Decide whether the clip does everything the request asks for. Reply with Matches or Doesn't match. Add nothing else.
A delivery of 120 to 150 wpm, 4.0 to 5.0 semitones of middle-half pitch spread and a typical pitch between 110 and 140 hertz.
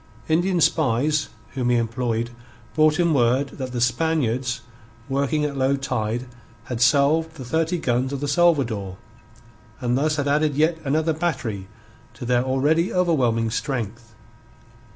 Matches